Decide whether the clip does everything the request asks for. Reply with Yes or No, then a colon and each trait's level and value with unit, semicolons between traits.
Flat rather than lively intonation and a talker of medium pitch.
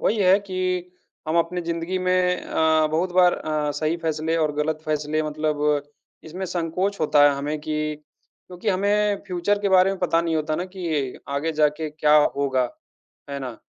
No: average, 3.2 semitones; medium, 160 Hz